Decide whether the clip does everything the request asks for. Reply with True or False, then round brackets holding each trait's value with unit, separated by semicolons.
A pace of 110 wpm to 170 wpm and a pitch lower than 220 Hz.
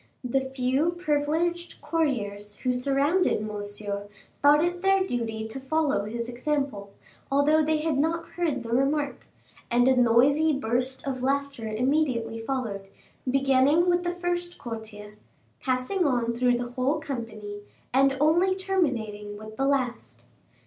False (135 wpm; 265 Hz)